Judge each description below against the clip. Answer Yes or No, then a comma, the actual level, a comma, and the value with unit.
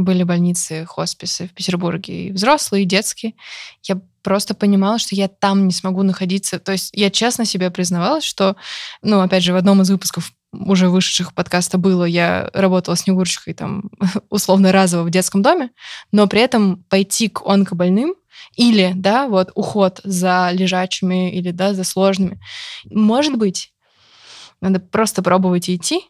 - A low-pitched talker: No, high, 190 Hz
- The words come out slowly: No, average, 155 wpm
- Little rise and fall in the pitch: Yes, narrow, 1.9 semitones